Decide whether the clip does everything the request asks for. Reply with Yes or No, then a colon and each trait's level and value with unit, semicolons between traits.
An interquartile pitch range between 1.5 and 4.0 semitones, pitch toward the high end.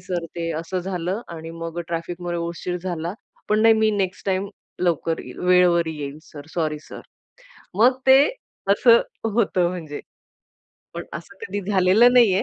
No: average, 3.2 semitones; medium, 180 Hz